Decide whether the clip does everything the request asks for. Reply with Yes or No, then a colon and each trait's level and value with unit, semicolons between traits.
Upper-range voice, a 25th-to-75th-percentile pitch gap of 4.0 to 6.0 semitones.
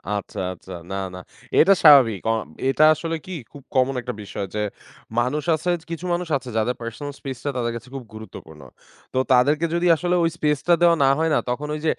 No: low, 135 Hz; average, 5.2 semitones